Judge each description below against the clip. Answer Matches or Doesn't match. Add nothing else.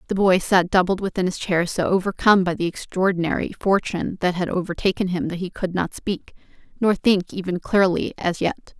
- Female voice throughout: Matches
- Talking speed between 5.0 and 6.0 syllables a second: Matches